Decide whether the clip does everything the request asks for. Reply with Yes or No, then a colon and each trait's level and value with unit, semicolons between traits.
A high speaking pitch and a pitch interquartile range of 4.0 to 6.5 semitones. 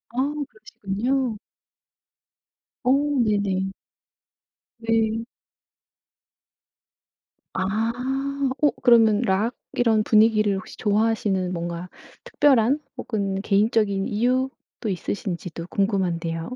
No: high, 215 Hz; average, 2.9 semitones